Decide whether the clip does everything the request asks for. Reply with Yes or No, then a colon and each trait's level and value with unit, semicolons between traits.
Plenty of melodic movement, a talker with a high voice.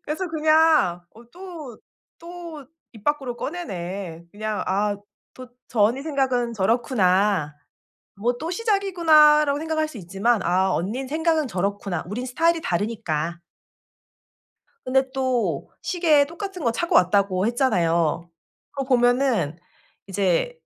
Yes: wide, 8.0 semitones; high, 245 Hz